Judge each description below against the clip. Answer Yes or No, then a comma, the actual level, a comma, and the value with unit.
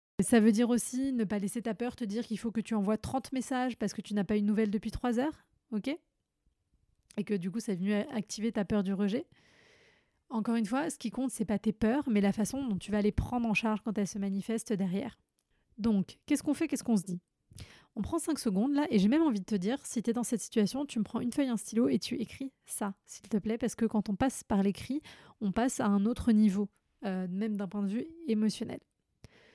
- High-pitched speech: Yes, high, 220 Hz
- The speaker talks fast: Yes, fast, 260 wpm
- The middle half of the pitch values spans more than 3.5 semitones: No, average, 3.0 semitones